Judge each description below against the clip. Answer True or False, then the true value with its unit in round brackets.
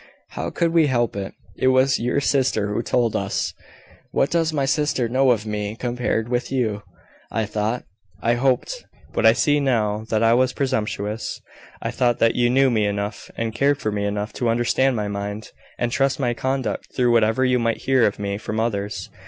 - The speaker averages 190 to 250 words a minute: True (195 wpm)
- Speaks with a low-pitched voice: True (120 Hz)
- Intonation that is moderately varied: True (3.6 semitones)